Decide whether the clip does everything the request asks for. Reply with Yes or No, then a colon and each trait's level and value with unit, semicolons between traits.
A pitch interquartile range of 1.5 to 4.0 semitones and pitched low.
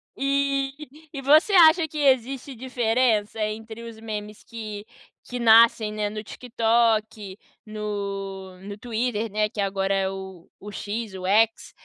No: average, 3.4 semitones; high, 220 Hz